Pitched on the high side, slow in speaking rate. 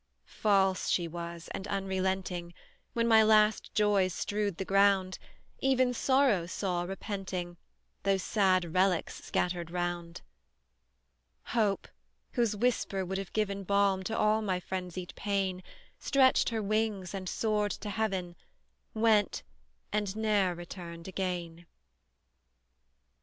Yes: high, 195 Hz; slow, 115 wpm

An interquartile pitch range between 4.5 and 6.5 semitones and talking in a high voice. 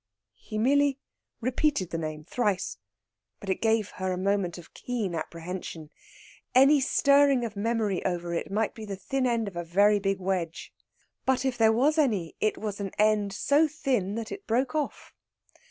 Yes: average, 5.2 semitones; high, 210 Hz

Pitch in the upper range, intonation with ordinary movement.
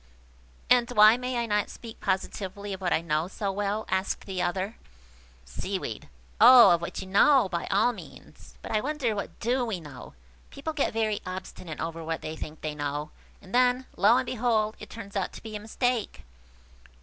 Yes: high, 205 Hz; average, 4.6 semitones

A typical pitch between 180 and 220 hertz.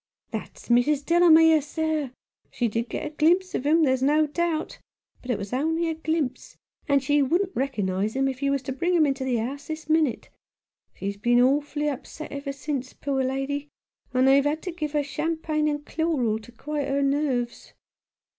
No: very high, 285 Hz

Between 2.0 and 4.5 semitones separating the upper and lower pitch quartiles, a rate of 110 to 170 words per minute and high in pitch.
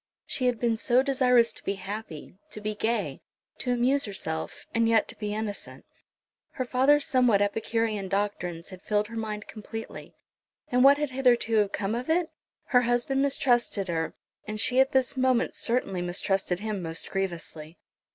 Yes: average, 4.0 semitones; average, 165 wpm; high, 225 Hz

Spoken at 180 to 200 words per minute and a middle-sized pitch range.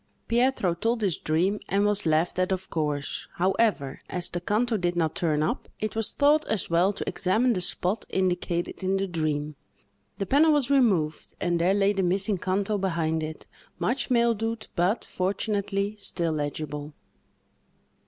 No: average, 165 wpm; average, 4.1 semitones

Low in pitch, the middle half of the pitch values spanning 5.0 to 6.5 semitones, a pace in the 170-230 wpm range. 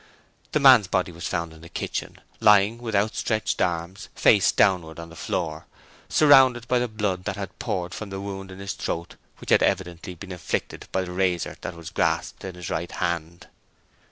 No: very low, 95 Hz; average, 3.4 semitones; average, 190 wpm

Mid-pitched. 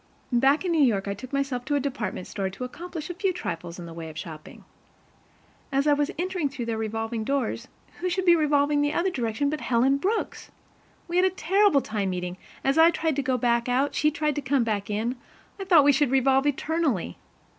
No: very high, 275 Hz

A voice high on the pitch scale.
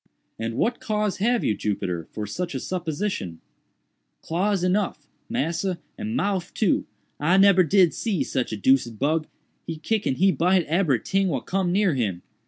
No: medium, 175 Hz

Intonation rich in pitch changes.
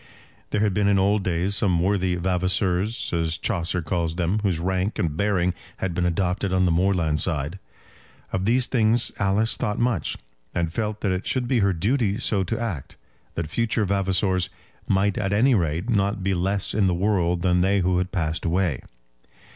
No: average, 2.8 semitones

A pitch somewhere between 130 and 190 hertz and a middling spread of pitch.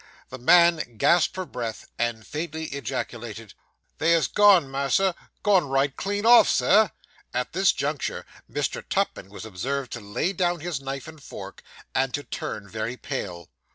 No: medium, 140 Hz; wide, 6.5 semitones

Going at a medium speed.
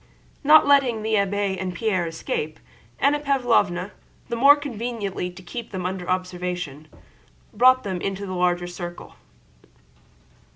No: slow, 130 wpm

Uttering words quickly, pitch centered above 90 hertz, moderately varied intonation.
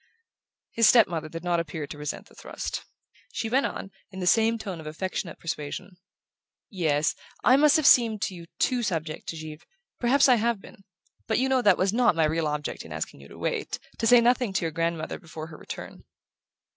No: fast, 210 wpm; medium, 185 Hz; wide, 6.3 semitones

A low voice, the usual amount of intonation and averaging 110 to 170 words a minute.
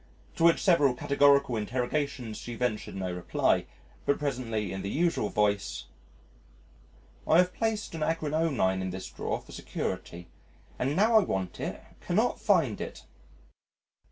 No: low, 130 Hz; wide, 7.8 semitones; average, 140 wpm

